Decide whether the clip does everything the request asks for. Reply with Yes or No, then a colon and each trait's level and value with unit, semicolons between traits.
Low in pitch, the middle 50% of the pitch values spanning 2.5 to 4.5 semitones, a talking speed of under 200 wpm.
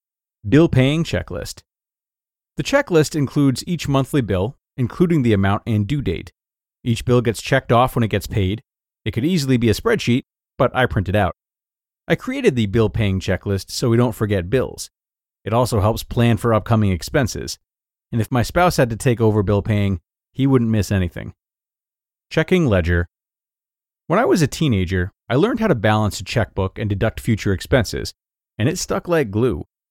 No: low, 115 Hz; average, 5.2 semitones; average, 180 wpm